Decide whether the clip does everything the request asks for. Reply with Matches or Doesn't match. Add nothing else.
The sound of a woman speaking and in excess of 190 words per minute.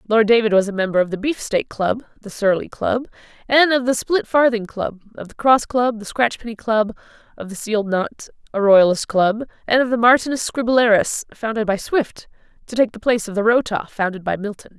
Matches